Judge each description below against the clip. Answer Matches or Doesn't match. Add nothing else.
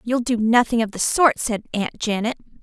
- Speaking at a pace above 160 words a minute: Matches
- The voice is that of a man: Doesn't match